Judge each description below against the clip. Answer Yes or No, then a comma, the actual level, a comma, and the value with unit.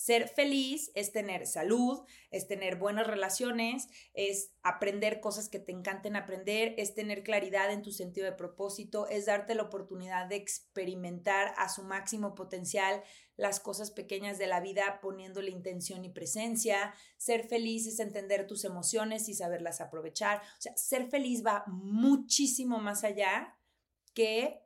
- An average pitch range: No, narrow, 2.3 semitones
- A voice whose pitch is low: No, high, 205 Hz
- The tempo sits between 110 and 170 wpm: Yes, average, 150 wpm